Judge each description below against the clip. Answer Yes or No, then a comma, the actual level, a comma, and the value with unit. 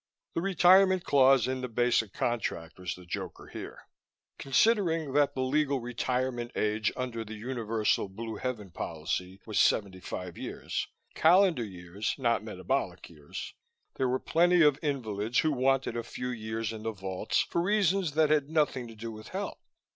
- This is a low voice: Yes, low, 120 Hz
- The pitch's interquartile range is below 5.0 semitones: No, wide, 5.4 semitones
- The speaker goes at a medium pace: Yes, average, 160 wpm